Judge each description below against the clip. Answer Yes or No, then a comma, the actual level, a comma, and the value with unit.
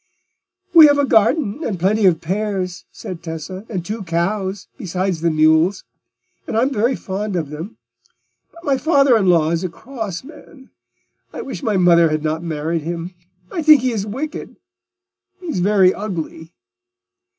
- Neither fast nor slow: Yes, average, 165 wpm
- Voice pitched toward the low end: No, high, 190 Hz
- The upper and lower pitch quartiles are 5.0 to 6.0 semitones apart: Yes, wide, 5.6 semitones